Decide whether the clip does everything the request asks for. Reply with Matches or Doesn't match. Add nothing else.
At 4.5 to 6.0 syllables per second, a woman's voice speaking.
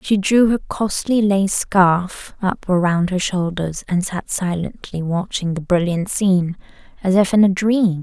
Doesn't match